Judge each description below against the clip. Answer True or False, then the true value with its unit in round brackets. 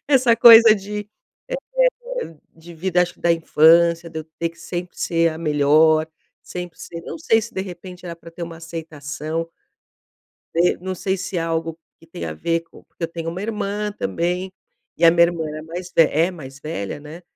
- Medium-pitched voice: True (170 Hz)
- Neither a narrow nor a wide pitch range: False (2.2 semitones)